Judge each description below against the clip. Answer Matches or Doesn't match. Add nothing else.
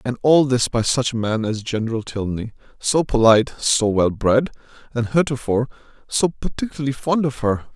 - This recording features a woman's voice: Doesn't match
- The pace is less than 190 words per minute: Matches